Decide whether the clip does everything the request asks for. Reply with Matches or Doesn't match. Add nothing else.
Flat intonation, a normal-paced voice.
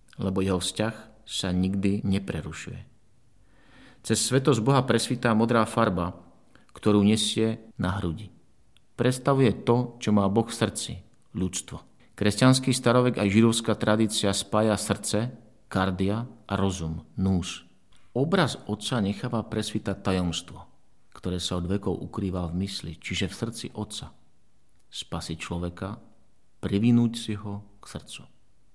Doesn't match